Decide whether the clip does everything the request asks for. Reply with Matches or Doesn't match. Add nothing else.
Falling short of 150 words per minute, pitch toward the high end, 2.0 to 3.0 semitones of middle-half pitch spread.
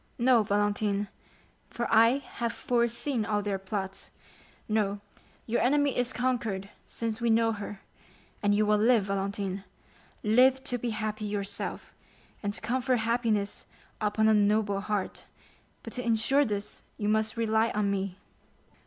Matches